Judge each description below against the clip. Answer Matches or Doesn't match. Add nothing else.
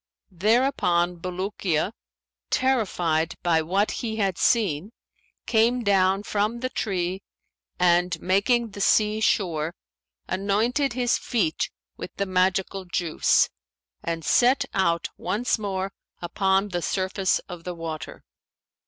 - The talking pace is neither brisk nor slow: Doesn't match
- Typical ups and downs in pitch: Matches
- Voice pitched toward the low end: Doesn't match